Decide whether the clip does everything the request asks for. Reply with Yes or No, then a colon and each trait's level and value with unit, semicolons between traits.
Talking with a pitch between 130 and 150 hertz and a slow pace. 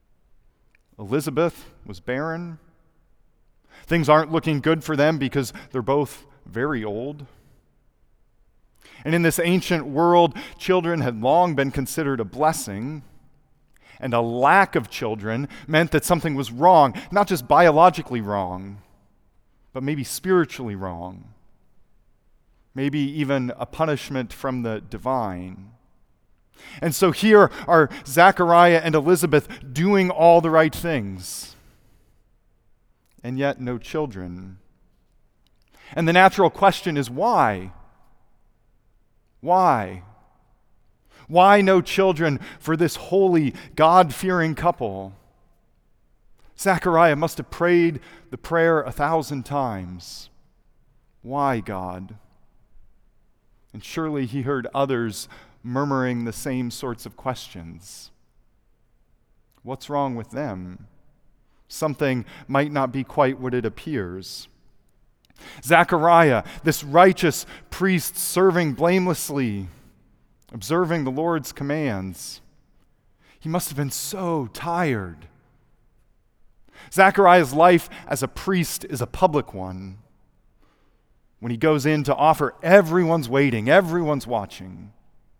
Yes: medium, 140 Hz; slow, 105 wpm